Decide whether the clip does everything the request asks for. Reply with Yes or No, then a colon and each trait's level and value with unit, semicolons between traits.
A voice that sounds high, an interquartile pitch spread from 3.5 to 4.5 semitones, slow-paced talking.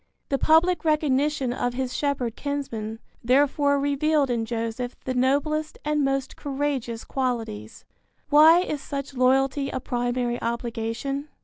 No: very high, 270 Hz; average, 3.0 semitones; slow, 125 wpm